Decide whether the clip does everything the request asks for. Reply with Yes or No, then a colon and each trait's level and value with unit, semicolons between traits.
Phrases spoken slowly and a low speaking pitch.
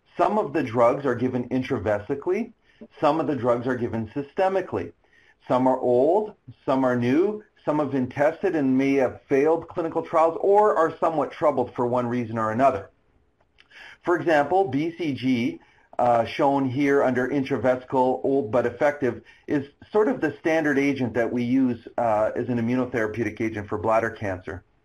No: average, 160 wpm; low, 130 Hz